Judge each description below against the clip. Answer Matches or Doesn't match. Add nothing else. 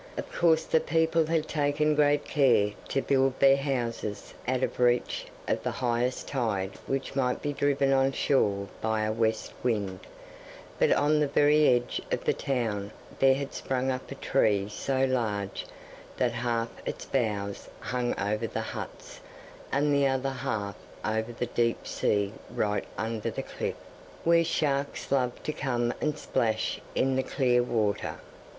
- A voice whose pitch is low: Matches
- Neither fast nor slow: Matches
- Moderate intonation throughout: Matches